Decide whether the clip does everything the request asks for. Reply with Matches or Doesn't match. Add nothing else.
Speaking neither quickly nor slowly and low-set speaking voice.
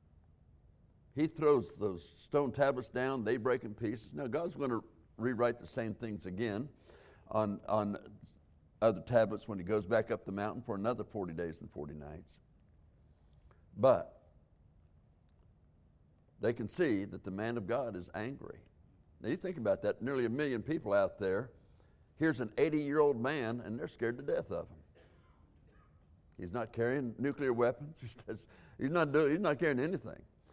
Matches